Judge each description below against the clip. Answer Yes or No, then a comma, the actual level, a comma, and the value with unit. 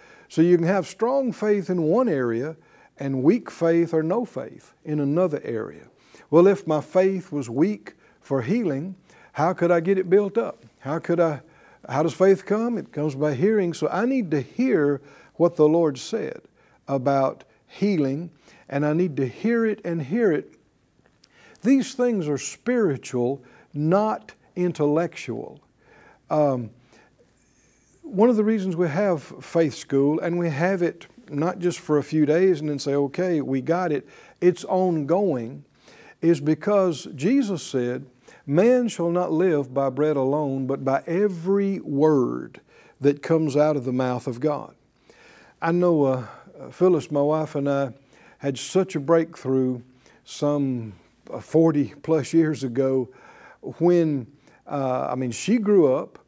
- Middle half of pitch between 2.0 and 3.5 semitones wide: No, average, 4.8 semitones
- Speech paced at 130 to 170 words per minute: Yes, average, 155 wpm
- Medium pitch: Yes, medium, 160 Hz